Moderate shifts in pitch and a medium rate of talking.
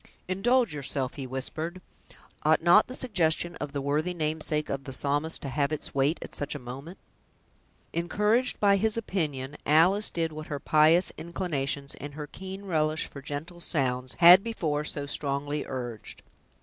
Yes: average, 3.8 semitones; average, 160 wpm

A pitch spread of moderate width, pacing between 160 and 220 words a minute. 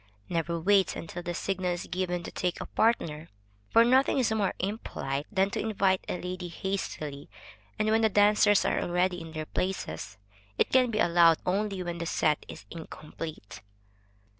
Yes: average, 3.4 semitones; average, 170 wpm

